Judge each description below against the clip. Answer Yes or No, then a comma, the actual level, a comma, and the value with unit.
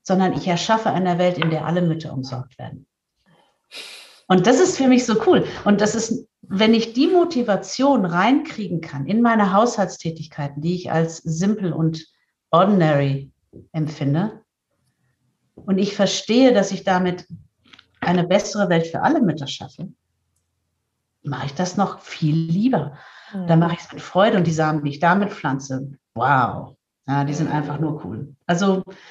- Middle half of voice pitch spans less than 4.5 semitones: No, average, 5.1 semitones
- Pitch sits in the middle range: Yes, medium, 175 Hz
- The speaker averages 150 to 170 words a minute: Yes, average, 160 wpm